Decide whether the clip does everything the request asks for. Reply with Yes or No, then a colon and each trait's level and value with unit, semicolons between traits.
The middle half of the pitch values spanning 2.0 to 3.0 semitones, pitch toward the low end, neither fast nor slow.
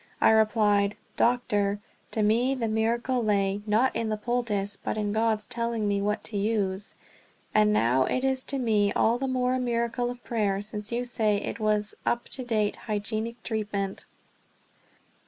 No: narrow, 2.5 semitones; high, 220 Hz; average, 170 wpm